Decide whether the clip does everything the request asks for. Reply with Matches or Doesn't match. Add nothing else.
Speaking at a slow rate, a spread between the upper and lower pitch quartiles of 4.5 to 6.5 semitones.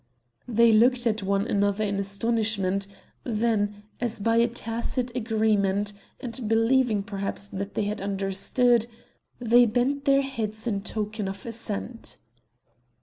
Doesn't match